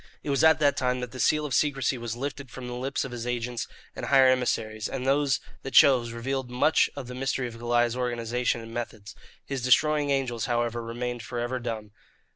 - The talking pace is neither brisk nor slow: No, fast, 210 wpm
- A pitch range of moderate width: No, narrow, 2.3 semitones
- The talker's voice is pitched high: No, low, 125 Hz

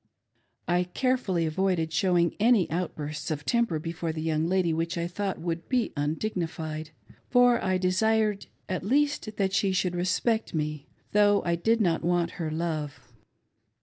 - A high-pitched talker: No, medium, 175 Hz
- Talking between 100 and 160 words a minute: Yes, average, 150 wpm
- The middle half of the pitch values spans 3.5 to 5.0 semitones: Yes, average, 4.0 semitones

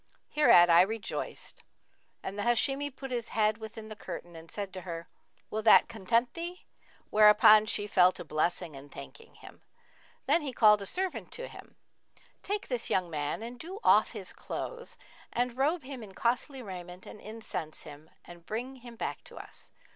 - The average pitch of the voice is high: Yes, high, 220 Hz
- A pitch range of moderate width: No, wide, 5.8 semitones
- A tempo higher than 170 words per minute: Yes, average, 185 wpm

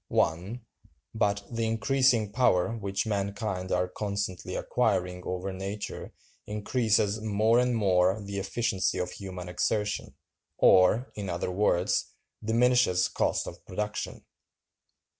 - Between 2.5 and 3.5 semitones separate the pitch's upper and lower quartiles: Yes, average, 3.2 semitones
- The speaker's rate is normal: No, slow, 115 wpm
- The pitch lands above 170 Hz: No, low, 100 Hz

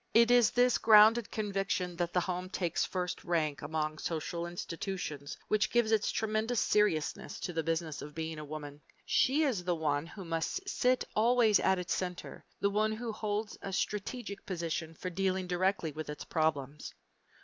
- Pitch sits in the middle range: Yes, medium, 180 Hz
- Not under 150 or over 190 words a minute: Yes, average, 170 wpm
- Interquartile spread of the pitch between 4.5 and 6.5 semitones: Yes, average, 4.9 semitones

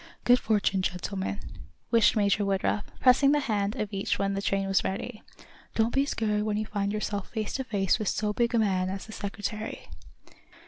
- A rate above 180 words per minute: Yes, average, 190 wpm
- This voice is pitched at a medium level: No, high, 210 Hz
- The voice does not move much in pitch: Yes, narrow, 2.0 semitones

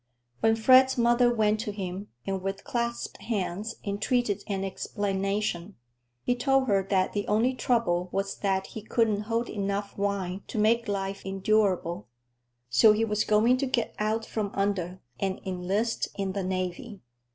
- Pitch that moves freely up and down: No, average, 2.8 semitones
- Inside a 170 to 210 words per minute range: No, average, 155 wpm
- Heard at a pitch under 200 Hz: No, high, 205 Hz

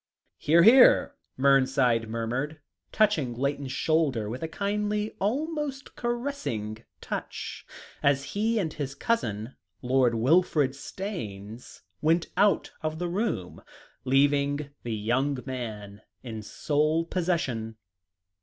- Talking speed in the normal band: No, slow, 105 wpm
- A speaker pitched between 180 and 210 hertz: No, medium, 140 Hz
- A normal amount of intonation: No, wide, 7.3 semitones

